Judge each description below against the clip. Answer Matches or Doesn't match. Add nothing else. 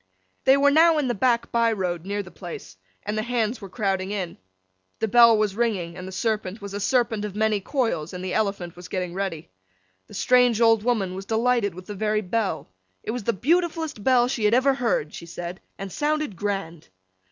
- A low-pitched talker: Doesn't match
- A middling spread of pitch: Matches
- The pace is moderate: Doesn't match